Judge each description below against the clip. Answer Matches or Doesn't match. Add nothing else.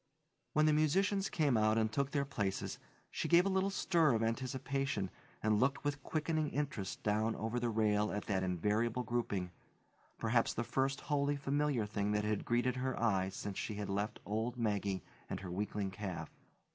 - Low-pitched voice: Matches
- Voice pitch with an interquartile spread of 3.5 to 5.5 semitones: Matches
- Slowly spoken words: Doesn't match